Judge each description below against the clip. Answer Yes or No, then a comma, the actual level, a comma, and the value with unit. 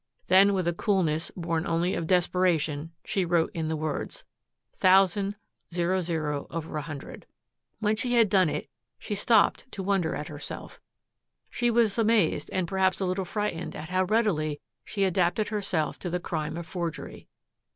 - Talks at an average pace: Yes, average, 150 wpm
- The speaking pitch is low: No, medium, 180 Hz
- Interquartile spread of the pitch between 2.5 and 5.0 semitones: Yes, average, 3.5 semitones